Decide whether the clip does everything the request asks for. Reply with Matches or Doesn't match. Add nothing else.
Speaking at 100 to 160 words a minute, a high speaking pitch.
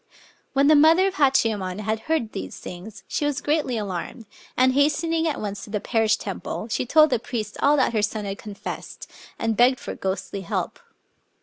Doesn't match